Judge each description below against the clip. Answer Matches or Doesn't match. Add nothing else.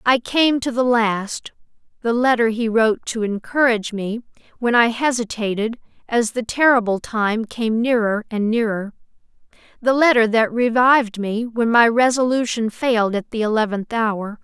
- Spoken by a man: Doesn't match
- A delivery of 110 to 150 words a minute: Matches